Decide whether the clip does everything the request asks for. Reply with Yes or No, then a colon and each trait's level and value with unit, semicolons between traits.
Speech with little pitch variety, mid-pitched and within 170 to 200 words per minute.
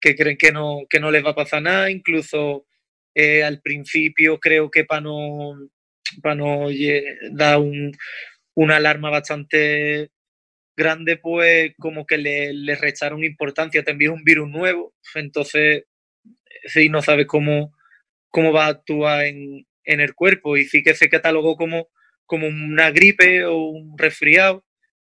No: narrow, 1.4 semitones; medium, 150 Hz; average, 155 wpm